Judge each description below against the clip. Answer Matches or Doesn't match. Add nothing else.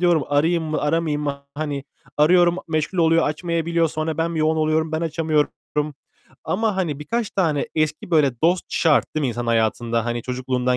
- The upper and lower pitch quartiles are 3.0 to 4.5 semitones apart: Doesn't match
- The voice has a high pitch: Doesn't match